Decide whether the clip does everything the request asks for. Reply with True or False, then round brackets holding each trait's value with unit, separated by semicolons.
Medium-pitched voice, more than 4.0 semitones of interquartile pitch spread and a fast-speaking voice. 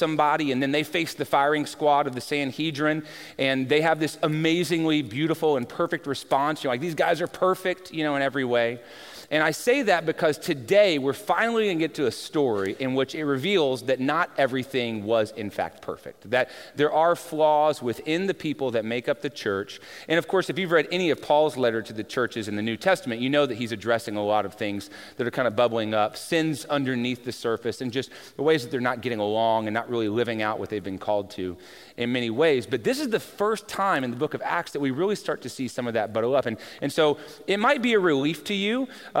True (145 Hz; 5.2 semitones; 245 wpm)